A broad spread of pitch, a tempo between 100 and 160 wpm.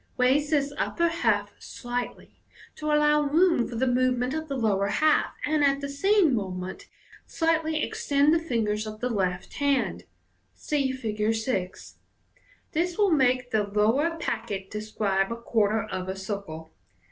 Yes: wide, 6.0 semitones; average, 155 wpm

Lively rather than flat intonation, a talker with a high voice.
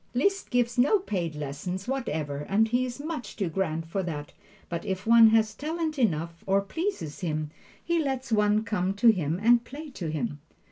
Yes: wide, 7.3 semitones; high, 210 Hz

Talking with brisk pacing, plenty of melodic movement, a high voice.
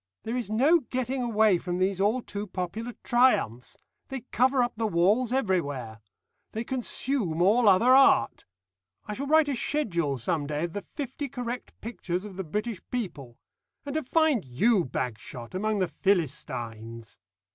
No: average, 155 wpm; wide, 6.8 semitones; high, 210 Hz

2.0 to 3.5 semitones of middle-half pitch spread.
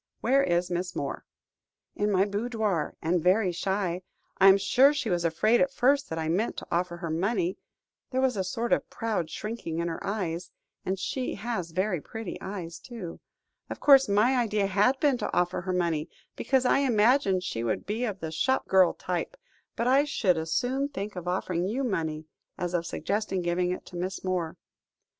No: average, 5.0 semitones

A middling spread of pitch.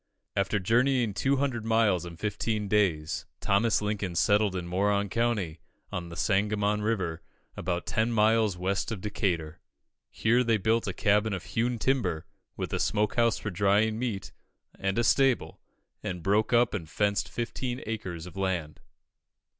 Yes: average, 3.4 semitones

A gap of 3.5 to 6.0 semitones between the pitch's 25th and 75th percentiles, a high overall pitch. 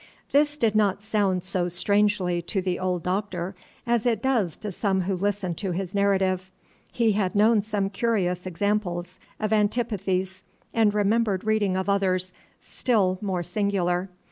No: narrow, 2.4 semitones; high, 200 Hz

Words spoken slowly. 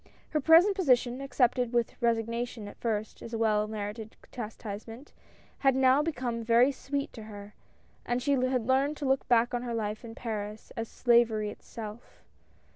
No: average, 165 wpm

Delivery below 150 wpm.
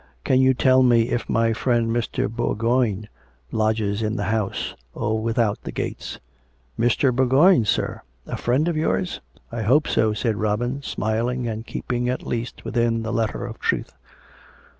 No: average, 180 wpm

